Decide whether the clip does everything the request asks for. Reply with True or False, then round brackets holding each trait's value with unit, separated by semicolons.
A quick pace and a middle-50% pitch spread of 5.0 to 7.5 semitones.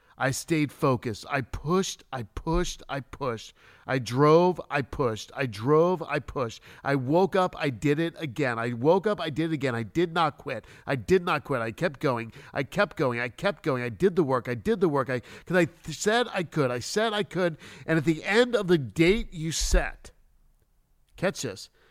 True (215 wpm; 5.5 semitones)